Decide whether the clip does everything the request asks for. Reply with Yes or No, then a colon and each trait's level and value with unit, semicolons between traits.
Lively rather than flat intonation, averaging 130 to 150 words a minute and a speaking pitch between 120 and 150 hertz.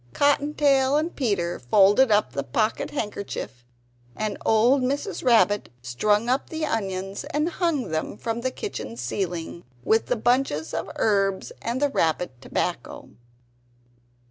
No: wide, 6.3 semitones; average, 140 wpm; high, 215 Hz